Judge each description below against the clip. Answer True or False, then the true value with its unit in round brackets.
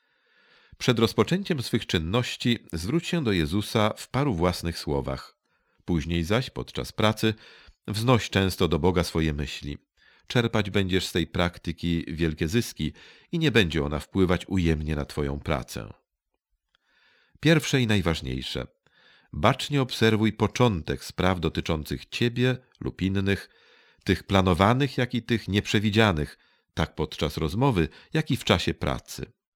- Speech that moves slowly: False (130 wpm)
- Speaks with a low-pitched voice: True (95 Hz)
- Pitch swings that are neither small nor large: False (6.4 semitones)